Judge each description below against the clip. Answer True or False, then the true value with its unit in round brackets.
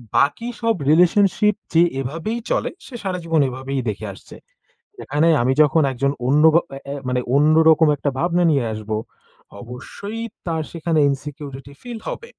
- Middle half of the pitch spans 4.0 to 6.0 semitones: True (4.4 semitones)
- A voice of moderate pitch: True (155 Hz)